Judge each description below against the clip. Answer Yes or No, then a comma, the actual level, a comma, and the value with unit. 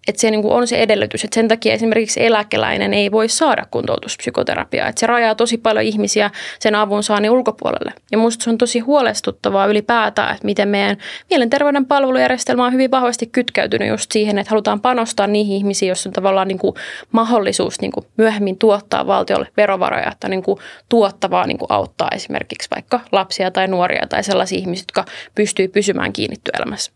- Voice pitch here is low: No, high, 215 Hz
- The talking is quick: Yes, fast, 180 wpm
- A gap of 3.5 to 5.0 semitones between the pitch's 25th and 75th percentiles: No, average, 2.8 semitones